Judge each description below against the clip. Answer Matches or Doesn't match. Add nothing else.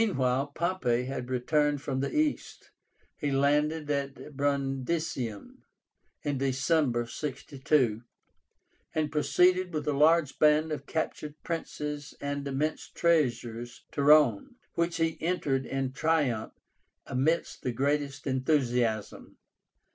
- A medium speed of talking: Doesn't match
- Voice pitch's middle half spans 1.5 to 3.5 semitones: Matches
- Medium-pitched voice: Matches